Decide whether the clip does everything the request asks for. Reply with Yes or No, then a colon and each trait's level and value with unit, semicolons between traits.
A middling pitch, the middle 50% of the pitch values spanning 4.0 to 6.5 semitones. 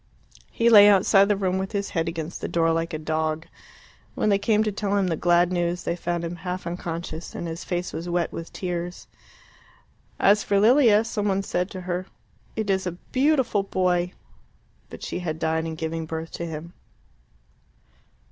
No: medium, 180 Hz; average, 3.1 semitones